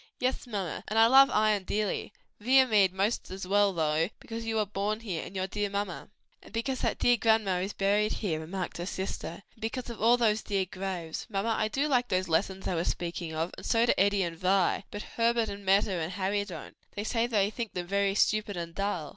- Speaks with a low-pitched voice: No, high, 200 Hz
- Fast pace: Yes, fast, 220 wpm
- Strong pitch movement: No, average, 3.1 semitones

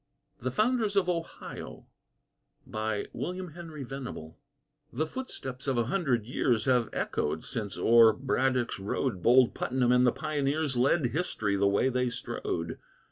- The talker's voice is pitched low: Yes, low, 125 Hz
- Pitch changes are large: No, average, 5.0 semitones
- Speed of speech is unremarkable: No, slow, 125 wpm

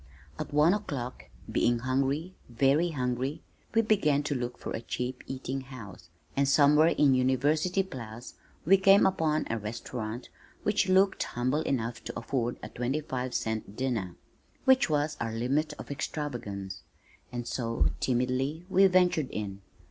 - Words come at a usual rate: Yes, average, 150 wpm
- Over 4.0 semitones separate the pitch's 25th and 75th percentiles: Yes, average, 4.4 semitones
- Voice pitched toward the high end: No, low, 135 Hz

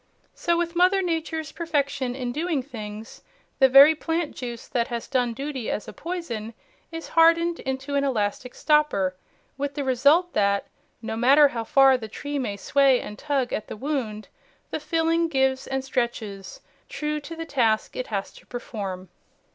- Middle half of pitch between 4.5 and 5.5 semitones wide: Yes, average, 4.9 semitones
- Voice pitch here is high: Yes, very high, 270 Hz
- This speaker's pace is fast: No, average, 170 wpm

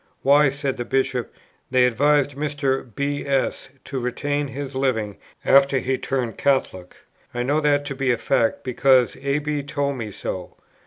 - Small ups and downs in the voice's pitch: Yes, narrow, 2.2 semitones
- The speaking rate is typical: Yes, average, 165 wpm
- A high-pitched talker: No, low, 135 Hz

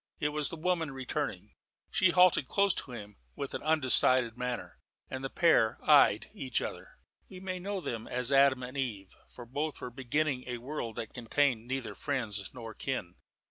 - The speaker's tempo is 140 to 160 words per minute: No, average, 180 wpm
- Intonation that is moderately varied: Yes, average, 4.2 semitones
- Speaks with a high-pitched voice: No, low, 130 Hz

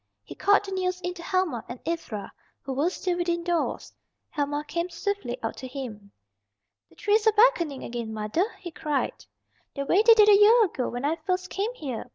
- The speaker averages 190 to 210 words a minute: Yes, average, 200 wpm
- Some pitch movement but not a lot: No, wide, 6.5 semitones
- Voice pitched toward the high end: Yes, very high, 340 Hz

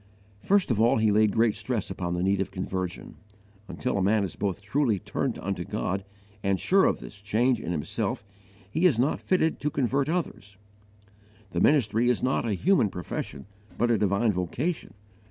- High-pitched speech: No, low, 110 Hz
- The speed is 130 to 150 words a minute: No, average, 180 wpm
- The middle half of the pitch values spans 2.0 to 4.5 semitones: No, average, 5.0 semitones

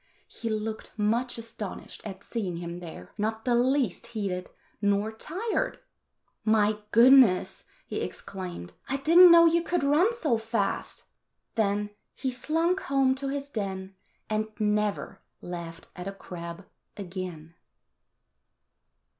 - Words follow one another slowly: Yes, slow, 130 wpm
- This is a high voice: Yes, high, 215 Hz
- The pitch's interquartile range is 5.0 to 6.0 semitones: Yes, wide, 5.6 semitones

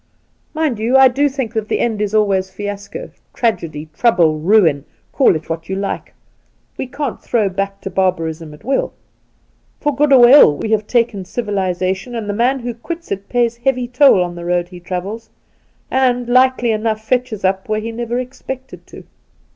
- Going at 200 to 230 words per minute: No, average, 185 wpm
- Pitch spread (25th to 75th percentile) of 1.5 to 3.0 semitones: No, average, 4.7 semitones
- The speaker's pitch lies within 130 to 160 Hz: No, high, 220 Hz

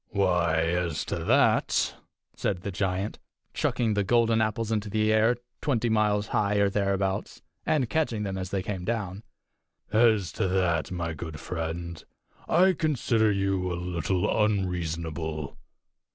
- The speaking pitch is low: Yes, low, 100 Hz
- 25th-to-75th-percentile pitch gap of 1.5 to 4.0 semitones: Yes, average, 3.7 semitones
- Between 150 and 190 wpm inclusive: No, average, 140 wpm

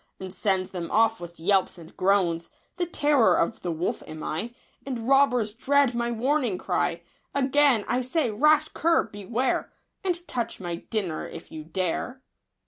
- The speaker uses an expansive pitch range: Yes, wide, 6.7 semitones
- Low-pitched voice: No, high, 225 Hz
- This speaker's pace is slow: No, average, 160 wpm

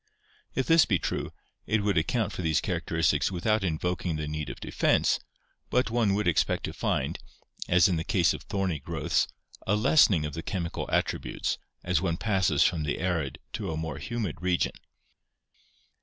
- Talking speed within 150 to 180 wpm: Yes, average, 170 wpm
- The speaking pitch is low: Yes, very low, 90 Hz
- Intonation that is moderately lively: Yes, average, 4.1 semitones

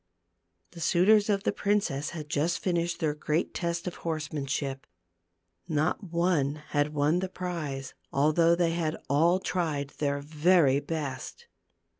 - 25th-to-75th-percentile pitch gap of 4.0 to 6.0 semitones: No, average, 3.2 semitones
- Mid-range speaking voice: Yes, medium, 160 Hz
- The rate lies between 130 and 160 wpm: Yes, average, 155 wpm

